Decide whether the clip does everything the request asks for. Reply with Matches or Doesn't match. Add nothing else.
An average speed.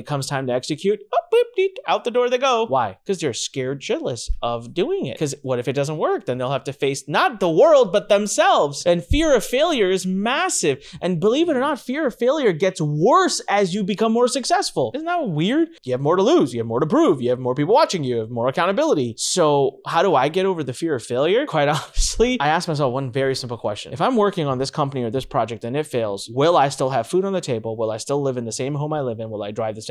Doesn't match